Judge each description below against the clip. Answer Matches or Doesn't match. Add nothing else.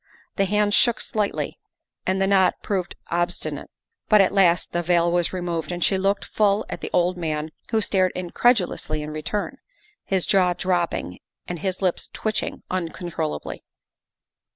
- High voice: Doesn't match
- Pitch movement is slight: Matches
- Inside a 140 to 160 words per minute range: Matches